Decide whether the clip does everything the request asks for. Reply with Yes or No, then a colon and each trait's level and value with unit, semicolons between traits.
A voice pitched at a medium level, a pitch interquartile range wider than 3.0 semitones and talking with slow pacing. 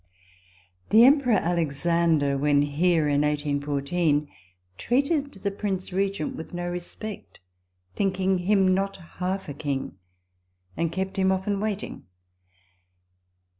Yes: medium, 180 Hz; average, 4.9 semitones; slow, 110 wpm